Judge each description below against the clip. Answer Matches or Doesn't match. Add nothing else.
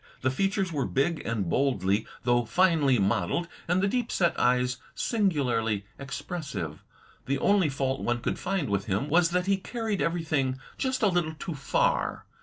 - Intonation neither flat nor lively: Doesn't match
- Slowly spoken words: Doesn't match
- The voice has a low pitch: Doesn't match